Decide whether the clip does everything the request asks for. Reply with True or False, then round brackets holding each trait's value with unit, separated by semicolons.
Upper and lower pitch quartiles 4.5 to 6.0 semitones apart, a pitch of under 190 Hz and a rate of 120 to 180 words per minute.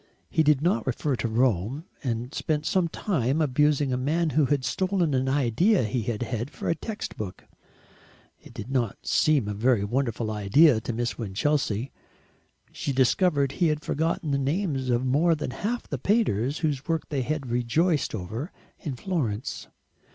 True (4.8 semitones; 135 Hz; 170 wpm)